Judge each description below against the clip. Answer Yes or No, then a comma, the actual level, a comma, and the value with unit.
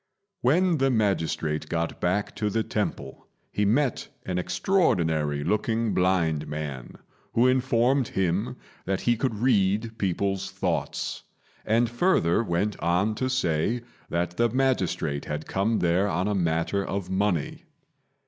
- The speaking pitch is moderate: No, low, 100 Hz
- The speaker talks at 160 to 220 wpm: No, slow, 135 wpm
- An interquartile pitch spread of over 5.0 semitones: Yes, wide, 5.5 semitones